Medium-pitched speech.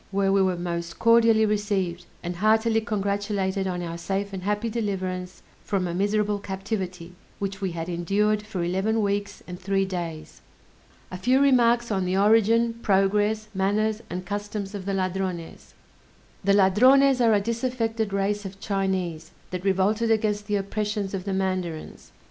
No: high, 200 Hz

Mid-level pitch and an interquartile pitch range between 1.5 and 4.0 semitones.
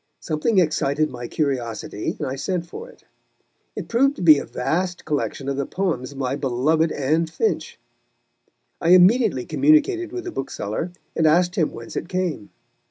No: medium, 160 Hz; wide, 5.4 semitones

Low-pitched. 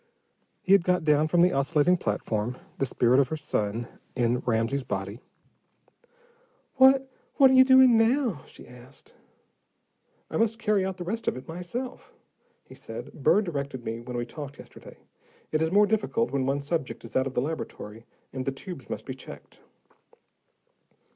No: medium, 150 Hz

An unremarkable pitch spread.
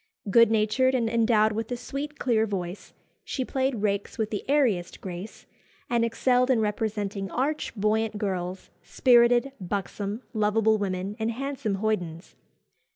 Yes: average, 3.2 semitones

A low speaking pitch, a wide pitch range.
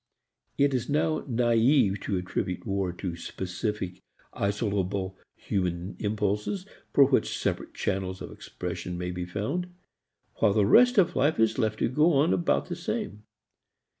Yes: low, 105 Hz; wide, 6.9 semitones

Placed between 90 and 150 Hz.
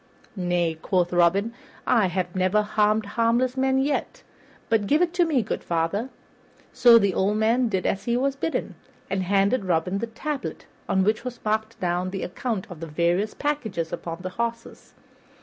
No: high, 210 Hz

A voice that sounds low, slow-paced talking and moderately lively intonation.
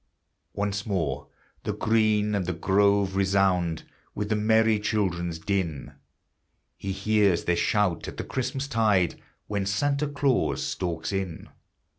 Yes: low, 100 Hz; slow, 130 wpm; average, 3.0 semitones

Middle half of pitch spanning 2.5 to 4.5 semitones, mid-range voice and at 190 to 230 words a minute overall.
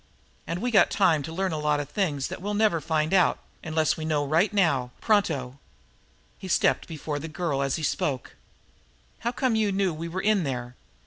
No: average, 4.9 semitones; medium, 160 Hz; average, 200 wpm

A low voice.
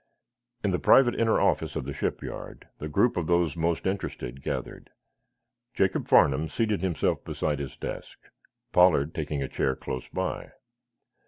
Yes: very low, 80 Hz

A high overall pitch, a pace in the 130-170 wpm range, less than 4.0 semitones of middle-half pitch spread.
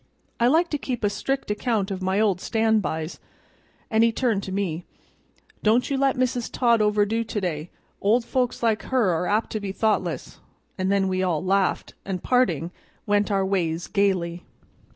No: high, 205 Hz; average, 180 wpm; average, 3.6 semitones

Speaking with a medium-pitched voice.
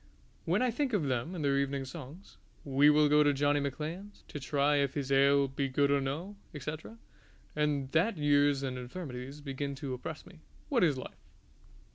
Yes: medium, 145 Hz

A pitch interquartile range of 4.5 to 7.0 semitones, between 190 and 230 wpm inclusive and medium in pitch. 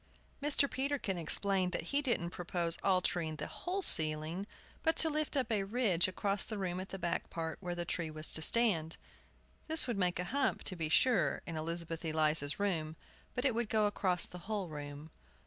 Yes: wide, 5.5 semitones; average, 195 wpm; medium, 180 Hz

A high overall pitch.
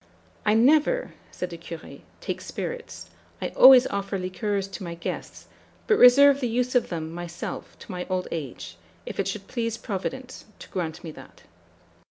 Yes: high, 200 Hz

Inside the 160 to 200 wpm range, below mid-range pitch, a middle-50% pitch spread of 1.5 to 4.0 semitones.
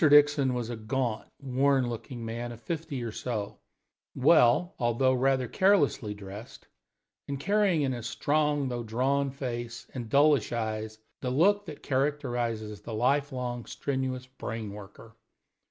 No: average, 140 wpm; low, 125 Hz; average, 3.4 semitones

